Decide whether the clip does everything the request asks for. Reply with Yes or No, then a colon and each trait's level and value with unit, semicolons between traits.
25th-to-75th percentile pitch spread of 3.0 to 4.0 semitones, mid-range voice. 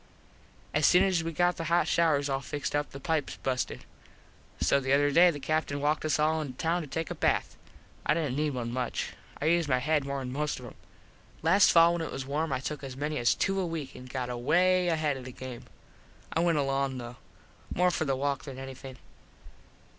Yes: average, 3.5 semitones; medium, 145 Hz